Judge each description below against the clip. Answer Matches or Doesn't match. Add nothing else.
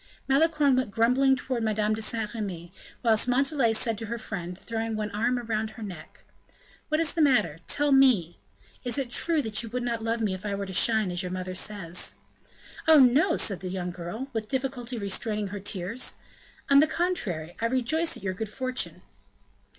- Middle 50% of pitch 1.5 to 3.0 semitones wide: Doesn't match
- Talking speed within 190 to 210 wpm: Matches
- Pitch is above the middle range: Matches